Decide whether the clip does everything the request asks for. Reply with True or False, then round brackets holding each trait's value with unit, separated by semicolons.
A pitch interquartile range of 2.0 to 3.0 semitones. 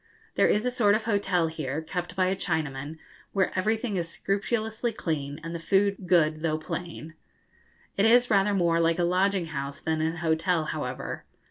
False (3.9 semitones)